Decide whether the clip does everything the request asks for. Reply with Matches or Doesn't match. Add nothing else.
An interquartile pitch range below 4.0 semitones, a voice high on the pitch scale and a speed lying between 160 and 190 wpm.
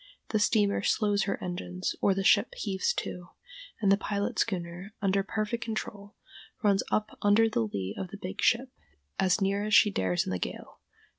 Matches